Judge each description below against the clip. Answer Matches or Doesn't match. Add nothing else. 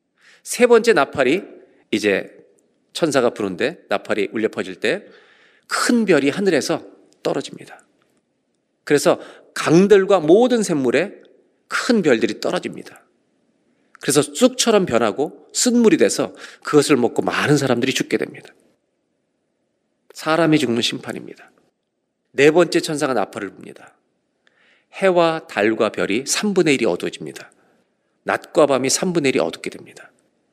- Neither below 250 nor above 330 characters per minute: Matches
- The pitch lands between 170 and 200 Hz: Matches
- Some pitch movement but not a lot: Doesn't match